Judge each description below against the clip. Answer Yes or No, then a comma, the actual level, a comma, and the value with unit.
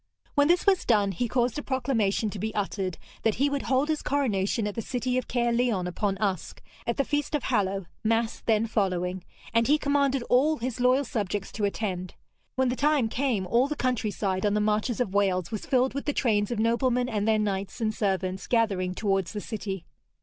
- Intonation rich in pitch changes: No, average, 4.3 semitones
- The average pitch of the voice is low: No, high, 225 Hz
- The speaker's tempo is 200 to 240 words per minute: Yes, fast, 205 wpm